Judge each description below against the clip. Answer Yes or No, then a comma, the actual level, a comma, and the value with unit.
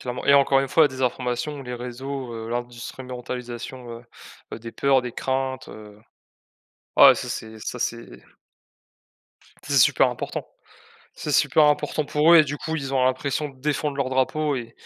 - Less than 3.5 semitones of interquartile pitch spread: Yes, narrow, 2.4 semitones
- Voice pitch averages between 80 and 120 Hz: No, low, 130 Hz